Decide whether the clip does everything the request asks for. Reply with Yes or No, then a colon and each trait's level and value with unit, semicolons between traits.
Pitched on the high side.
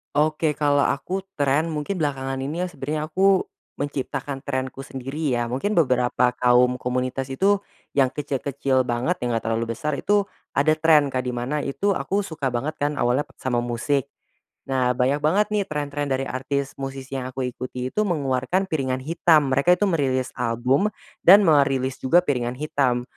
No: low, 135 Hz